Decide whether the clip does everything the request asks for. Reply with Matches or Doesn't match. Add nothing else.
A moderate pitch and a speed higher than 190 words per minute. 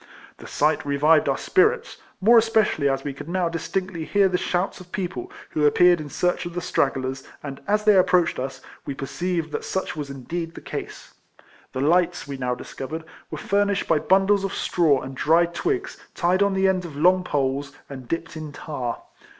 Matches